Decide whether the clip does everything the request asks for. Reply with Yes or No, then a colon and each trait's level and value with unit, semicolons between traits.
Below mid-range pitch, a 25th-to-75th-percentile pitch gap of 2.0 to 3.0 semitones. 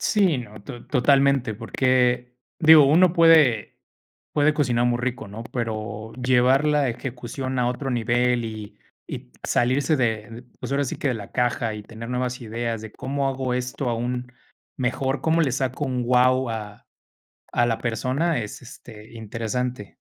Yes: low, 125 Hz; narrow, 2.6 semitones